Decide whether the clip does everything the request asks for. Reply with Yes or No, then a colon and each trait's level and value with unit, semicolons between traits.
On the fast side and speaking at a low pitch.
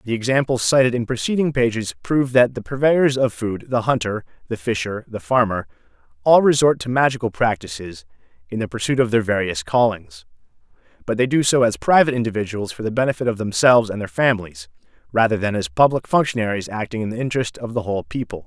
No: average, 180 wpm; low, 115 Hz